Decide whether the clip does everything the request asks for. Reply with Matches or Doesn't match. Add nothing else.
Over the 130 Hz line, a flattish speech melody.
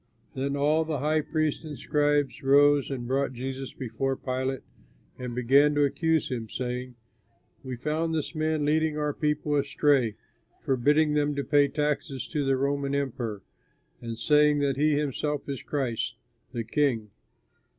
Matches